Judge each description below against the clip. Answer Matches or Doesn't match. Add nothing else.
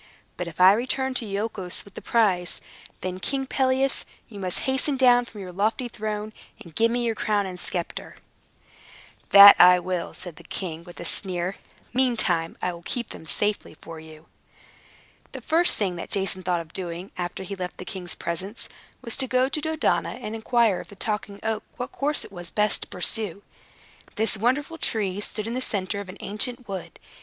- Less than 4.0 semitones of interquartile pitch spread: Doesn't match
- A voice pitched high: Matches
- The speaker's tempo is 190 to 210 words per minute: Matches